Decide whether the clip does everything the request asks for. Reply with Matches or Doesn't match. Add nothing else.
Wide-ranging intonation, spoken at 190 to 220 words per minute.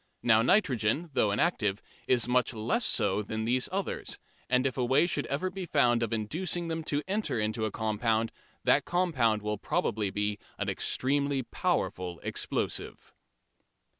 Doesn't match